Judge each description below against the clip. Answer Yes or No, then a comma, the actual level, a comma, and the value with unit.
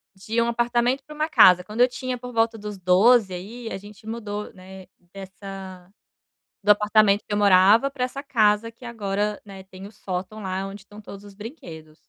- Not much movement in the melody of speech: No, average, 3.3 semitones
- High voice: Yes, high, 210 Hz